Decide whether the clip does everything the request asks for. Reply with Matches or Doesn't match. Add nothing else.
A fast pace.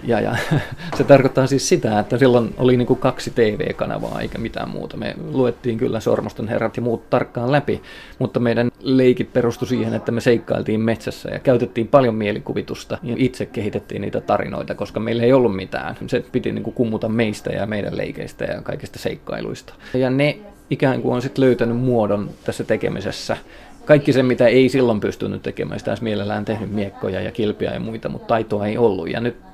Matches